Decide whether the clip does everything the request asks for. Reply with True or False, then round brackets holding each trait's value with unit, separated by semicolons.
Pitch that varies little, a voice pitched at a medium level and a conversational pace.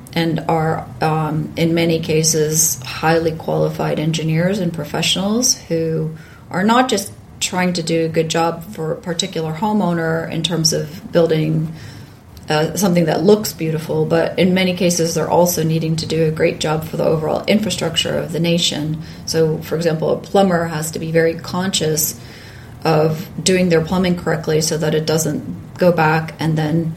True (1.4 semitones; 160 Hz; 170 wpm)